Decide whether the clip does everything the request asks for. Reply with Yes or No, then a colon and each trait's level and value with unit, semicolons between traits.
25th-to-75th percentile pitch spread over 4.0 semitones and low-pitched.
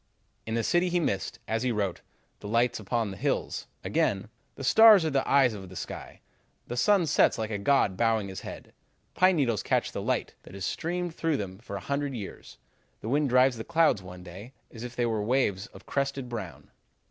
Yes: wide, 5.6 semitones; low, 120 Hz